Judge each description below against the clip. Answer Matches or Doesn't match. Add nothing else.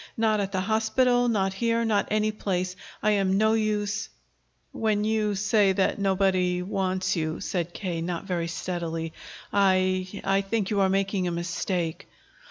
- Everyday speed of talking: Matches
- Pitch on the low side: Doesn't match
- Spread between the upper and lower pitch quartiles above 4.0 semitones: Doesn't match